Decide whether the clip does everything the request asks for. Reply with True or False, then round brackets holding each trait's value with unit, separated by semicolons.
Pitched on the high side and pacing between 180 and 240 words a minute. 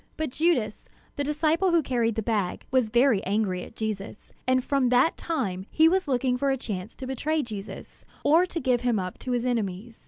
True (250 Hz; 205 wpm)